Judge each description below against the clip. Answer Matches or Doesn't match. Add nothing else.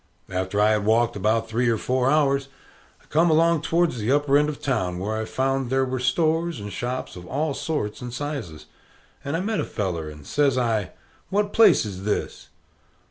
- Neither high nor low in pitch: Doesn't match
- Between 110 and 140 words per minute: Doesn't match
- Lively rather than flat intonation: Matches